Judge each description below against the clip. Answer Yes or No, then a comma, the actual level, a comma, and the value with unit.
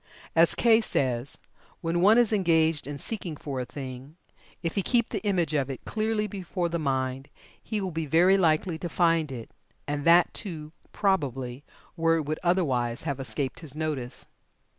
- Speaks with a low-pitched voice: No, medium, 160 Hz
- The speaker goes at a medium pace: Yes, average, 175 wpm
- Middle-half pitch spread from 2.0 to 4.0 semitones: No, average, 4.8 semitones